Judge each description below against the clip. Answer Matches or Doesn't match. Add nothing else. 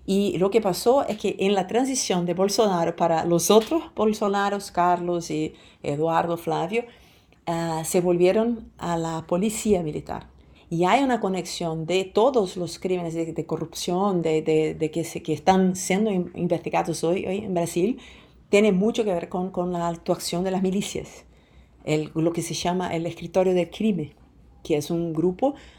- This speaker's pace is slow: Doesn't match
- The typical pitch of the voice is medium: Matches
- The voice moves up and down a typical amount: Matches